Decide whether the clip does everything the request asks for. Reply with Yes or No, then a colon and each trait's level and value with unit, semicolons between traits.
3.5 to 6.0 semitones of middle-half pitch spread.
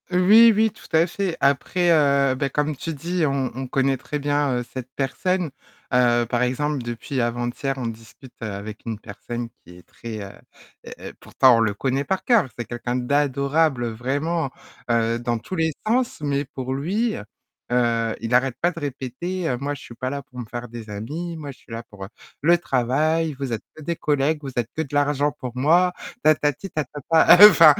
Yes: average, 4.7 semitones